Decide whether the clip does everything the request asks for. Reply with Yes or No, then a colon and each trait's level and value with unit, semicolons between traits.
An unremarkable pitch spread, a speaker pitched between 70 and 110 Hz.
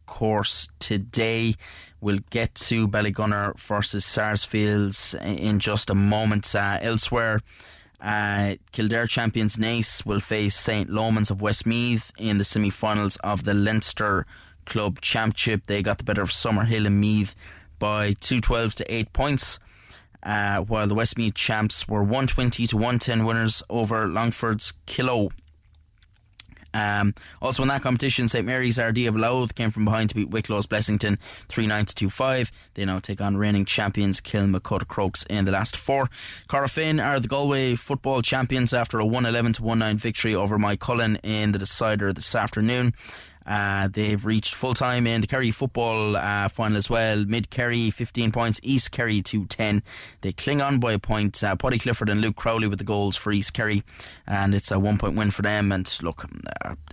No: narrow, 2.3 semitones; low, 105 Hz